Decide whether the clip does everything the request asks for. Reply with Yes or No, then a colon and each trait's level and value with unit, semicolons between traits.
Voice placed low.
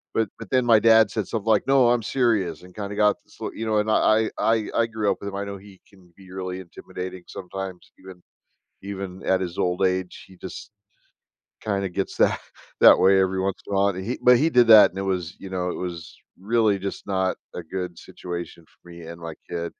Yes: very low, 95 Hz